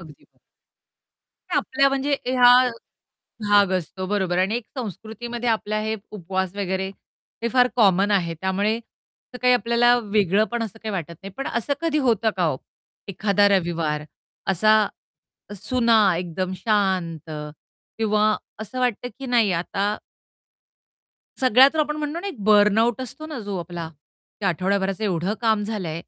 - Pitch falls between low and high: No, high, 210 Hz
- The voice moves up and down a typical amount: Yes, average, 4.1 semitones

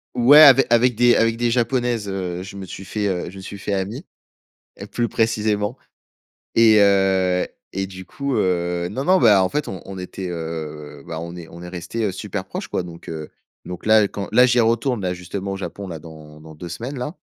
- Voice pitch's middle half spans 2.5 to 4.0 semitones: No, average, 4.6 semitones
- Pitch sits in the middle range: No, very low, 95 Hz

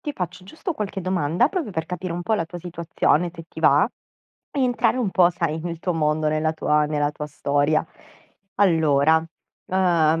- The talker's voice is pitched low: No, medium, 170 Hz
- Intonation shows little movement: No, average, 3.2 semitones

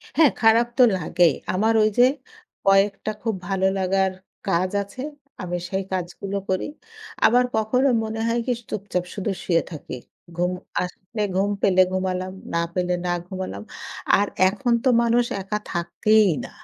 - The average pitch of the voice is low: No, high, 195 Hz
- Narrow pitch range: No, average, 3.0 semitones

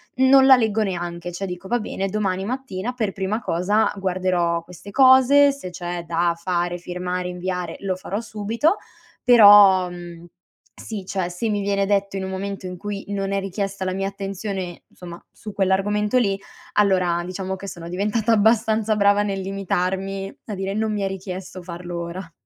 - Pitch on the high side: Yes, high, 195 Hz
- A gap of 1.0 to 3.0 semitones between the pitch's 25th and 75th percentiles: Yes, narrow, 2.5 semitones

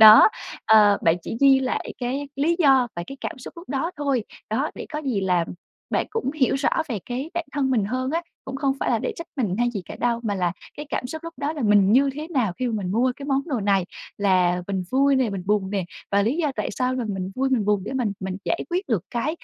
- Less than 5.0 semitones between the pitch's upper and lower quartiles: No, average, 5.3 semitones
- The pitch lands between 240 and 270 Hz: Yes, very high, 250 Hz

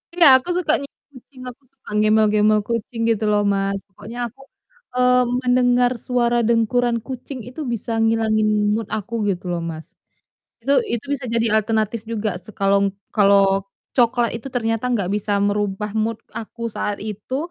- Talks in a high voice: Yes, high, 225 Hz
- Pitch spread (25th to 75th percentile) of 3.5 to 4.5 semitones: No, average, 3.0 semitones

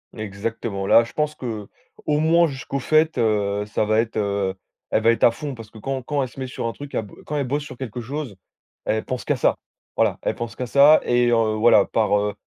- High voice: No, low, 115 Hz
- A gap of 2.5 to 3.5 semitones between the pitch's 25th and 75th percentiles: No, average, 4.3 semitones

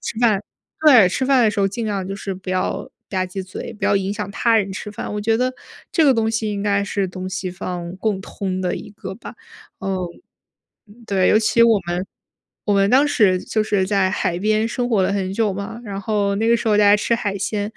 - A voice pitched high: Yes, high, 205 Hz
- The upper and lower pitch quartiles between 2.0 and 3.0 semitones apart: Yes, narrow, 2.6 semitones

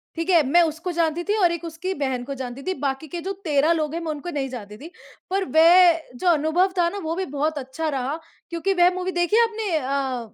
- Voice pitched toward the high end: Yes, very high, 325 Hz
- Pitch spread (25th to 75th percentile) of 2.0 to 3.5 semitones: No, average, 4.2 semitones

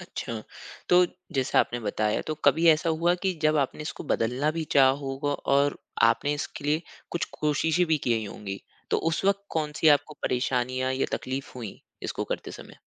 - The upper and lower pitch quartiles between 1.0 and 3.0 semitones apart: No, average, 4.0 semitones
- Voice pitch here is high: No, medium, 145 Hz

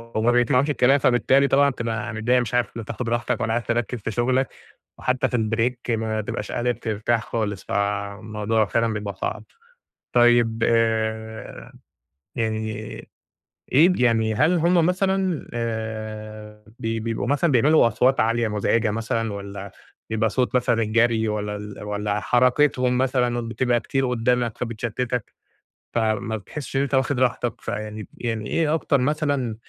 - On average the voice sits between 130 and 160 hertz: No, low, 115 Hz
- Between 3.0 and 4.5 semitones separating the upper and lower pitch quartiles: No, narrow, 2.6 semitones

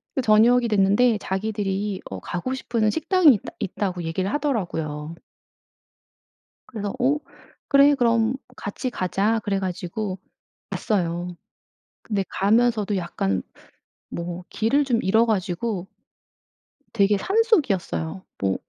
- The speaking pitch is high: Yes, high, 205 Hz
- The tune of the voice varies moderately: Yes, average, 4.3 semitones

